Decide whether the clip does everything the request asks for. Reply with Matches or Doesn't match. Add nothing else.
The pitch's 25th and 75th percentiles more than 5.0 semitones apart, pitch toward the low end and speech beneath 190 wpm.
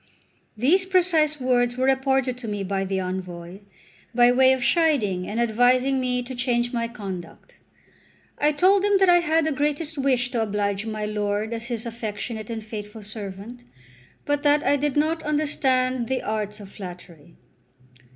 Doesn't match